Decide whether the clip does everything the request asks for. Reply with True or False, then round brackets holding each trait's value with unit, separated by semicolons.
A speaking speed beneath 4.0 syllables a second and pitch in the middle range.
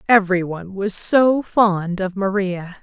False (3.8 syllables/s; 195 Hz)